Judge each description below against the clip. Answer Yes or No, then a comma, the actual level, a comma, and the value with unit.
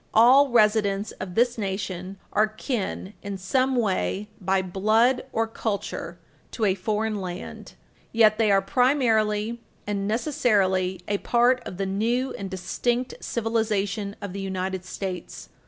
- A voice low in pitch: No, high, 210 Hz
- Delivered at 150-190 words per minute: No, average, 140 wpm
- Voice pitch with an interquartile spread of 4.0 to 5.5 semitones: No, average, 3.1 semitones